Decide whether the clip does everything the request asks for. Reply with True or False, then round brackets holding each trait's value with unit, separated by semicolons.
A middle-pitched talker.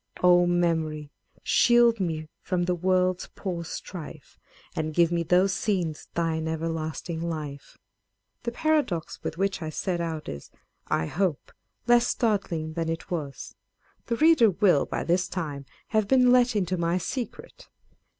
True (175 Hz)